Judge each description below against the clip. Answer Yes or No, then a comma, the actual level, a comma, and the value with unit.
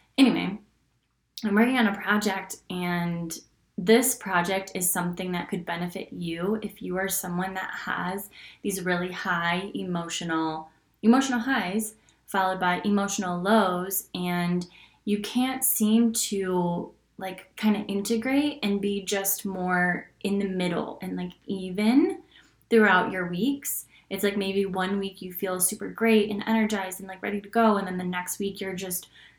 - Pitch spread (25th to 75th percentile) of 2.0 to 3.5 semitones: Yes, average, 2.9 semitones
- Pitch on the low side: No, high, 195 Hz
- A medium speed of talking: Yes, average, 155 wpm